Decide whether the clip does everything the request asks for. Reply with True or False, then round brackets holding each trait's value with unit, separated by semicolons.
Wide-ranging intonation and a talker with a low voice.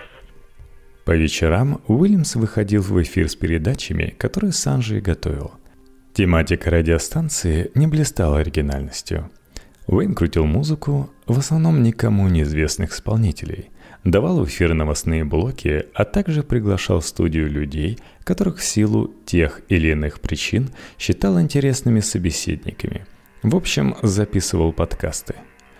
True (7.2 semitones; 95 Hz)